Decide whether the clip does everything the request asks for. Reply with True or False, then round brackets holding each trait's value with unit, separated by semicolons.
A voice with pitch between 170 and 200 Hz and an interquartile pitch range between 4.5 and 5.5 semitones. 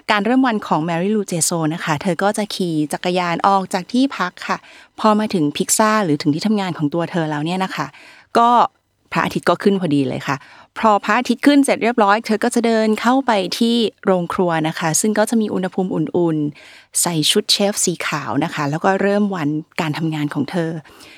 True (190 Hz; 4.9 semitones)